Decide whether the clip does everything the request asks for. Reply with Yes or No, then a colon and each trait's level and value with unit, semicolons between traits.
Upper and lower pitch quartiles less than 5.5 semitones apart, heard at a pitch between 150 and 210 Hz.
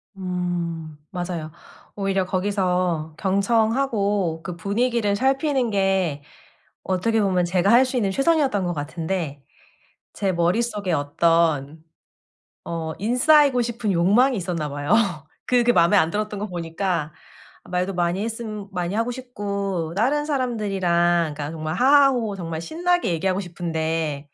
Yes: average, 5.1 semitones; high, 190 Hz